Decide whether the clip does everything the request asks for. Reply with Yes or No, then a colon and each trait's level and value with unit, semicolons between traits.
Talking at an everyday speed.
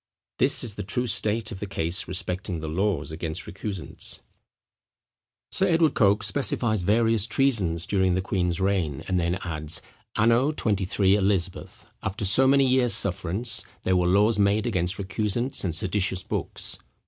Yes: average, 150 wpm